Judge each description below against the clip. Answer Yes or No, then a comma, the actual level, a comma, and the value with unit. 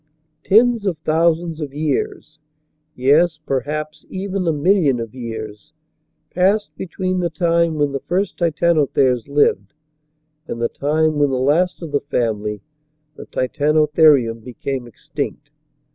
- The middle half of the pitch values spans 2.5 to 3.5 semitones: No, average, 4.4 semitones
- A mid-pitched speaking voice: Yes, medium, 150 Hz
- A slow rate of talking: Yes, slow, 130 wpm